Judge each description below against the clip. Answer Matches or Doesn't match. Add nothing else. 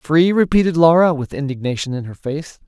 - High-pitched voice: Doesn't match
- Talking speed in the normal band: Matches